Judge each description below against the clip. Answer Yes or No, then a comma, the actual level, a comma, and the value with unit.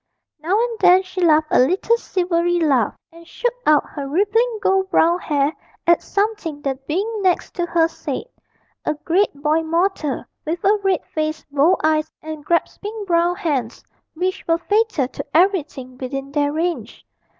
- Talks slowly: No, average, 160 wpm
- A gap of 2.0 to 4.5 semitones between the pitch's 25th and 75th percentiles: Yes, average, 4.0 semitones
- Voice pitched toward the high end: Yes, very high, 335 Hz